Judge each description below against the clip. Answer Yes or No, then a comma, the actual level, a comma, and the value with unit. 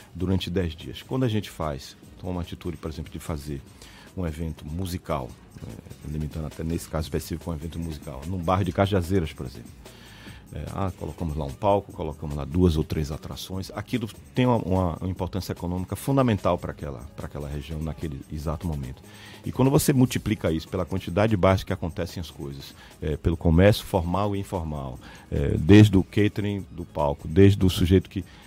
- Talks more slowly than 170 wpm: No, fast, 185 wpm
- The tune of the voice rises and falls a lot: No, average, 4.0 semitones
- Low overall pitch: Yes, very low, 90 Hz